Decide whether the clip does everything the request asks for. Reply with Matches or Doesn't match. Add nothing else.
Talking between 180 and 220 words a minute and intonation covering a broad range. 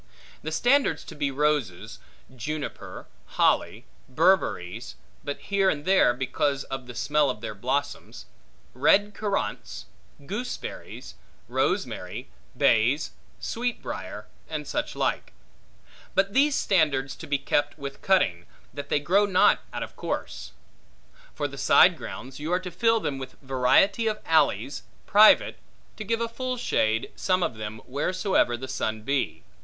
Doesn't match